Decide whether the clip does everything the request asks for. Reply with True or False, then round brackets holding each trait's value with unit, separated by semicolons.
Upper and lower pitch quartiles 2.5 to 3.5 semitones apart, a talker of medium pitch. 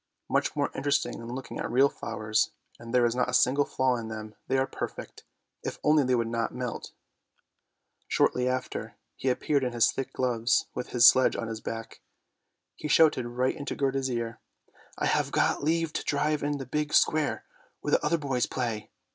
False (3.2 semitones; 125 Hz)